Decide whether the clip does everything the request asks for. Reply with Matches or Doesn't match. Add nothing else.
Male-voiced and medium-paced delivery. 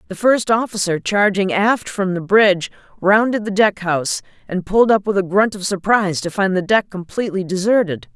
Doesn't match